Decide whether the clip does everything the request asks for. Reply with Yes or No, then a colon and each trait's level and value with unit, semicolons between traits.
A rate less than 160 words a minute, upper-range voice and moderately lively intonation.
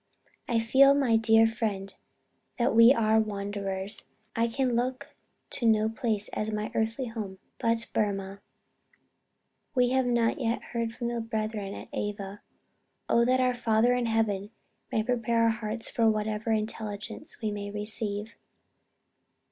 No: average, 145 wpm; high, 225 Hz; narrow, 1.9 semitones